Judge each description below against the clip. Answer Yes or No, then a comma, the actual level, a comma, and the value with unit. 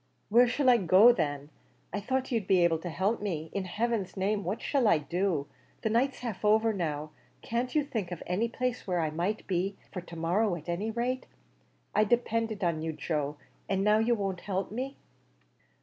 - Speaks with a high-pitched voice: Yes, high, 200 Hz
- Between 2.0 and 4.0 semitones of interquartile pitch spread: No, average, 5.0 semitones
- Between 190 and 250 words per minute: Yes, average, 195 wpm